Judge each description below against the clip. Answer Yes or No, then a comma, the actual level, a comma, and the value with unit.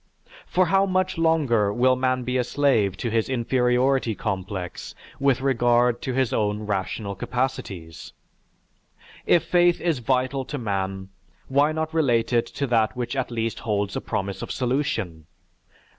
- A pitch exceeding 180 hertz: No, low, 125 Hz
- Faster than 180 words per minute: No, average, 150 wpm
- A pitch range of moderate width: Yes, average, 4.4 semitones